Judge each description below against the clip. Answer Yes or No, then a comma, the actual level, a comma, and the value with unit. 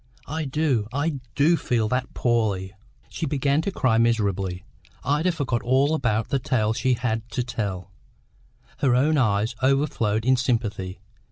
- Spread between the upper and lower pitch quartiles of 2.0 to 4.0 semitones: No, average, 4.4 semitones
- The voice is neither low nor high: No, low, 125 Hz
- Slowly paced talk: No, average, 150 wpm